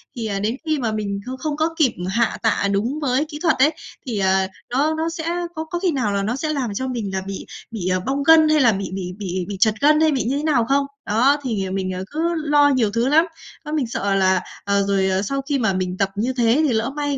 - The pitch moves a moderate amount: No, wide, 6.6 semitones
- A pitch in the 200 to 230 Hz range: No, high, 240 Hz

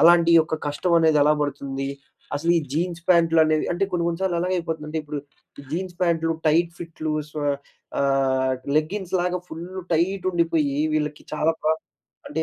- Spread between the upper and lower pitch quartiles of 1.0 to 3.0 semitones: Yes, narrow, 2.4 semitones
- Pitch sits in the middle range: Yes, medium, 165 Hz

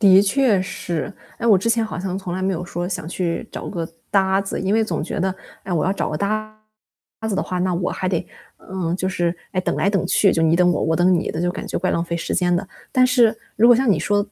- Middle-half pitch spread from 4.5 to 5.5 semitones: No, average, 2.7 semitones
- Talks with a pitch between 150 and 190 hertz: Yes, medium, 185 Hz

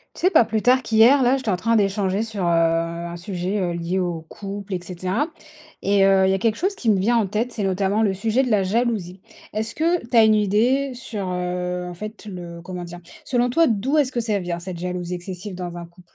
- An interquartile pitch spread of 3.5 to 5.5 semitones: Yes, average, 4.1 semitones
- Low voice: No, high, 195 Hz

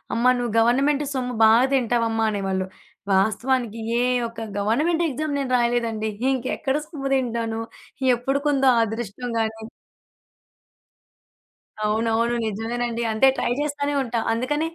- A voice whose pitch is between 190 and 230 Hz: No, high, 240 Hz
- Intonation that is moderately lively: Yes, average, 3.0 semitones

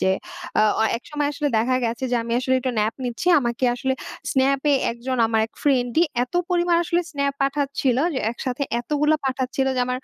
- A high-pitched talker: Yes, very high, 260 Hz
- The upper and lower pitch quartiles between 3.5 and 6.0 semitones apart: No, average, 2.8 semitones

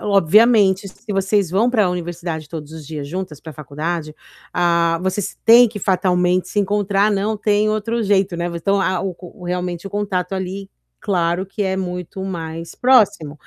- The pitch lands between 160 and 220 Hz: Yes, high, 190 Hz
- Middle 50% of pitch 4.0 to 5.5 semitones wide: No, average, 3.1 semitones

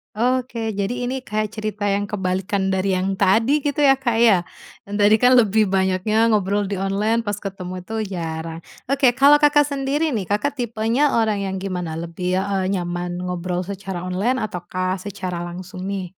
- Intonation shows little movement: No, average, 3.8 semitones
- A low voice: No, high, 200 Hz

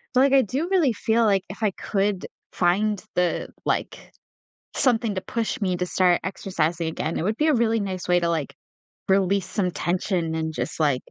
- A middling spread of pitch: Yes, average, 4.2 semitones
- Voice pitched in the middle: No, high, 195 Hz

